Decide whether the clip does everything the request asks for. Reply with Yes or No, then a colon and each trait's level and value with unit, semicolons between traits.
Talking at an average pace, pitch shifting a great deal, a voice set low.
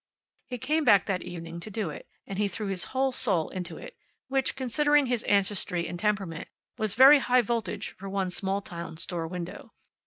No: average, 190 wpm; wide, 5.7 semitones; high, 200 Hz